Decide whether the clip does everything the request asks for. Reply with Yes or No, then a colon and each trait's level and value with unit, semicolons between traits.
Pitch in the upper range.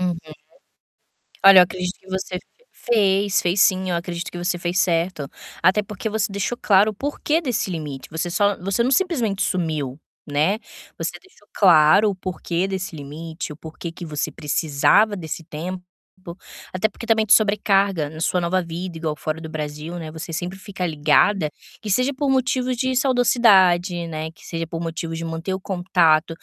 No: medium, 180 Hz